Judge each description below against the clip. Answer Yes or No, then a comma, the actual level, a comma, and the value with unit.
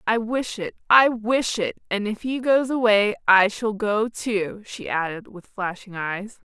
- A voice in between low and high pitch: No, high, 215 Hz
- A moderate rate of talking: Yes, average, 185 wpm